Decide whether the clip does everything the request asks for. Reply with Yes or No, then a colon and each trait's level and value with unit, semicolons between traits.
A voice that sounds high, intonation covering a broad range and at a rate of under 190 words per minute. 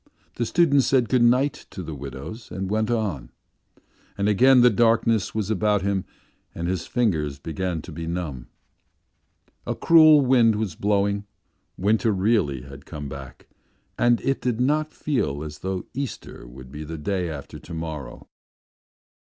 No: low, 100 Hz; wide, 7.2 semitones; average, 155 wpm